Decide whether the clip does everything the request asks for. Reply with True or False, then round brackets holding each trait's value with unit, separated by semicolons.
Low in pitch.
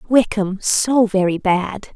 False (205 Hz)